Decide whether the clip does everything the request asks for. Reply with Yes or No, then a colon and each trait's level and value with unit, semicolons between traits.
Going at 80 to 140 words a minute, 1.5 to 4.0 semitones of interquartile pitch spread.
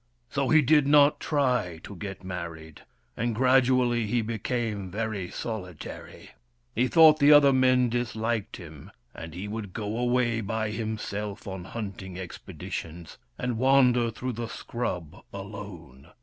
No: slow, 135 wpm; average, 4.5 semitones